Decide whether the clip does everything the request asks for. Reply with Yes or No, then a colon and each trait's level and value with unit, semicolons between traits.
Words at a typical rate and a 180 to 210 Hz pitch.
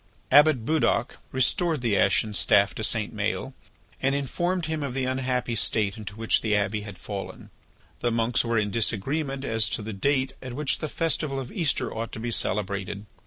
No: average, 185 wpm; low, 120 Hz